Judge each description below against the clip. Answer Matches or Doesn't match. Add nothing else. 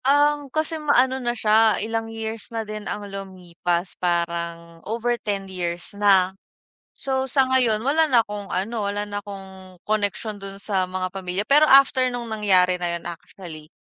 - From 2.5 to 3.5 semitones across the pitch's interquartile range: Doesn't match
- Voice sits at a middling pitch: Doesn't match